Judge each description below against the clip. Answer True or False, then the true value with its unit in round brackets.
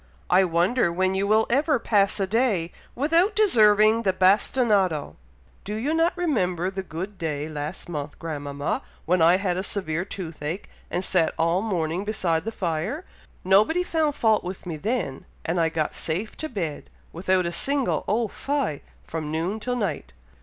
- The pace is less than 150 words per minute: False (165 wpm)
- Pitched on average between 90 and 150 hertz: False (190 Hz)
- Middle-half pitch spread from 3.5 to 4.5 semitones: False (5.3 semitones)